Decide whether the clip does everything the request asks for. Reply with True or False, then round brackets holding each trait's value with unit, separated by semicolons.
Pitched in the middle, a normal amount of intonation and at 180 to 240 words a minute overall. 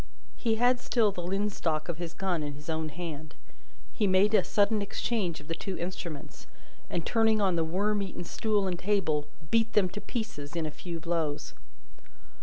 True (180 Hz; 4.4 semitones; 185 wpm)